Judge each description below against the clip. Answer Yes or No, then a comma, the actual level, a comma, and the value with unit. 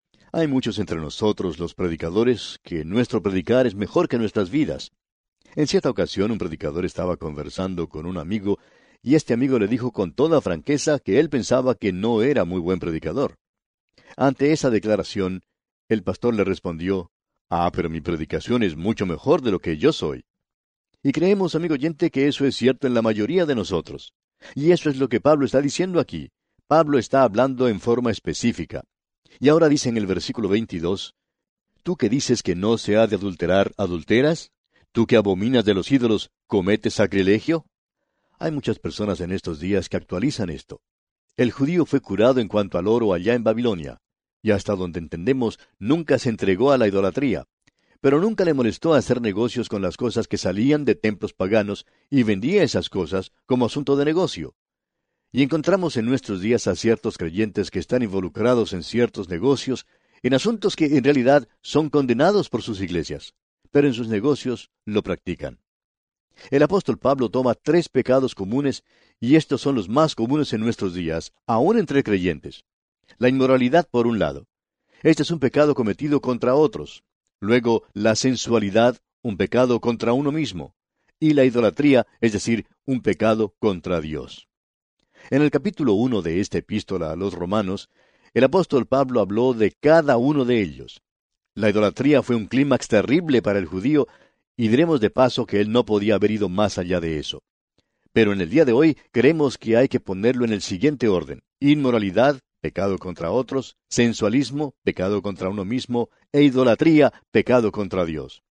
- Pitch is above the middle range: No, low, 115 Hz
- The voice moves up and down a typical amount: No, wide, 5.7 semitones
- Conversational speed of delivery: Yes, average, 175 wpm